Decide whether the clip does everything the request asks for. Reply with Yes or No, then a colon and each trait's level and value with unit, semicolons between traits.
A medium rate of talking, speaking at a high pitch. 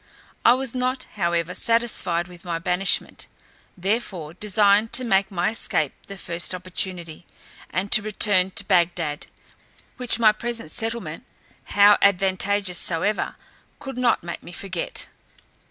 No: slow, 130 wpm; high, 195 Hz